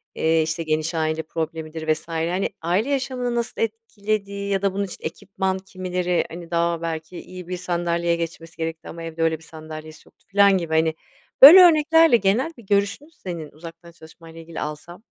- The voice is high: No, medium, 170 Hz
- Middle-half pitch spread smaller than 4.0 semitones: Yes, average, 3.6 semitones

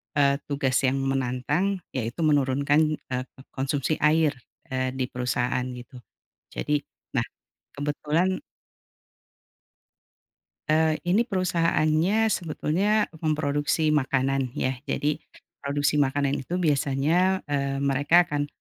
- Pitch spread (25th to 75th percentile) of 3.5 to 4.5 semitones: No, average, 3.0 semitones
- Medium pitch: Yes, medium, 145 Hz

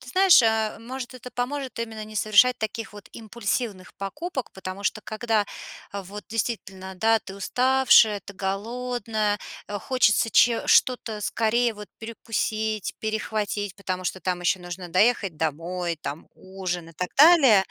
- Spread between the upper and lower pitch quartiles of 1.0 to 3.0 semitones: No, average, 3.7 semitones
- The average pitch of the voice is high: Yes, high, 215 Hz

